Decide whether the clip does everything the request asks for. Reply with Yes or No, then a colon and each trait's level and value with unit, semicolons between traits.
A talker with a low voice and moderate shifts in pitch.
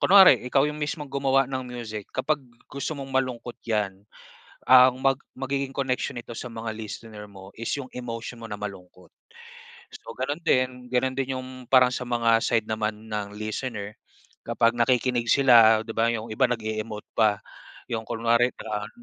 Yes: low, 120 Hz; average, 3.0 semitones